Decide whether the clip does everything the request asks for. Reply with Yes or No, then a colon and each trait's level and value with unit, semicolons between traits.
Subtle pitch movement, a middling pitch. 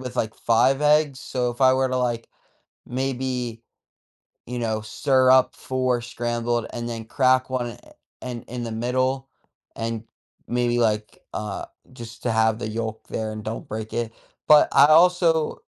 No: narrow, 2.3 semitones; low, 120 Hz